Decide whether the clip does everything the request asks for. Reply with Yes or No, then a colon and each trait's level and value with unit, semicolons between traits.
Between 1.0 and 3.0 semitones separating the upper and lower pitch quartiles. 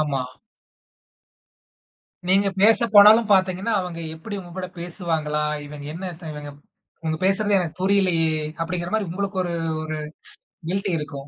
No: average, 3.8 semitones